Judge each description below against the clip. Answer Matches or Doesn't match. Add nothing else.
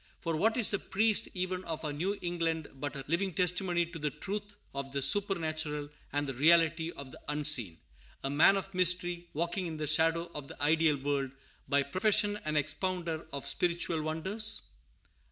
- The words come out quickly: Doesn't match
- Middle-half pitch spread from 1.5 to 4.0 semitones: Matches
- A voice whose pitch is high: Doesn't match